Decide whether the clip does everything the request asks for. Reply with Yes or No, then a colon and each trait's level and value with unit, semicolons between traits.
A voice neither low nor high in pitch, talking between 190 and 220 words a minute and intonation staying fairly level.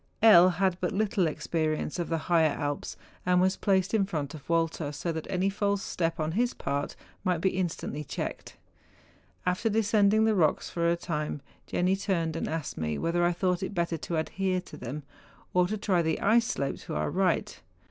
No: medium, 175 Hz; average, 200 wpm; average, 3.3 semitones